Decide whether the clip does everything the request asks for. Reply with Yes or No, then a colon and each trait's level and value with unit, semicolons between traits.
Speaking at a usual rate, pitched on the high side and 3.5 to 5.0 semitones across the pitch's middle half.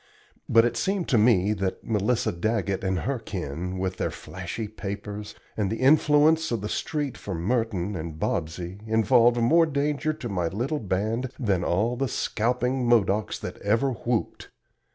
No: average, 160 wpm; low, 110 Hz; average, 4.6 semitones